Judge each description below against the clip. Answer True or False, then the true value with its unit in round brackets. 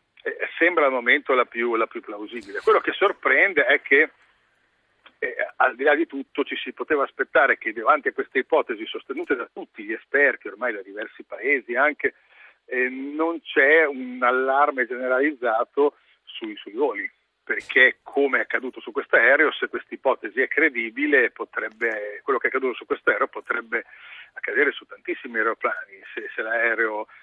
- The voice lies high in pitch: True (385 Hz)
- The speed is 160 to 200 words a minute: True (170 wpm)